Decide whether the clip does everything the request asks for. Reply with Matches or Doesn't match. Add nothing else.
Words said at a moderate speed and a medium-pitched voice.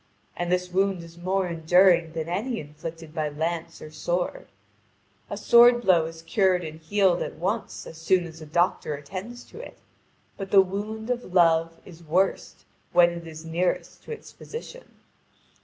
Matches